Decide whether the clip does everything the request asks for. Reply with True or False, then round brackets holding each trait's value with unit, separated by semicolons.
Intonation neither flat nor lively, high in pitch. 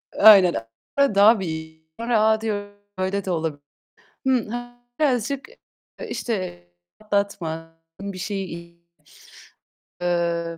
True (4.3 semitones; 195 Hz)